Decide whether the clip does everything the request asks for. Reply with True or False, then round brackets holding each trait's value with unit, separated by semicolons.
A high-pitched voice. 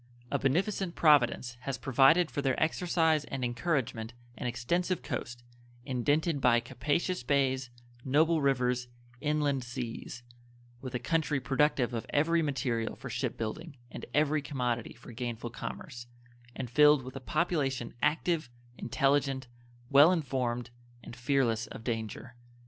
False (135 Hz)